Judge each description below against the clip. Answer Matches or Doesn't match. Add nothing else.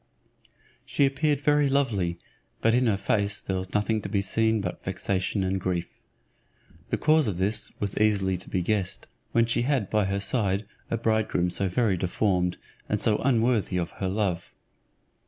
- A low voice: Matches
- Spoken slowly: Doesn't match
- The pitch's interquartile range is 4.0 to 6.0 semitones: Doesn't match